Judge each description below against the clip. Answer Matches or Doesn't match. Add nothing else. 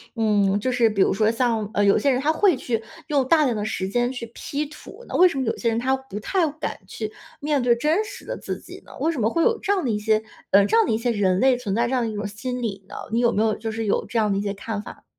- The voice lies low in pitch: Doesn't match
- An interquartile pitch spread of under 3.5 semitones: Doesn't match